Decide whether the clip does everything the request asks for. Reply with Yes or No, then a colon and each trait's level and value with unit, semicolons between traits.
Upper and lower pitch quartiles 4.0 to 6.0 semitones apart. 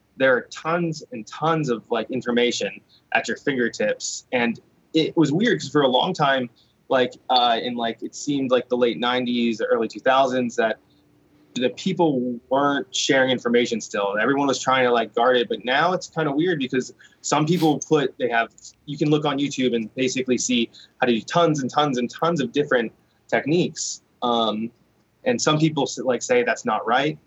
No: average, 3.6 semitones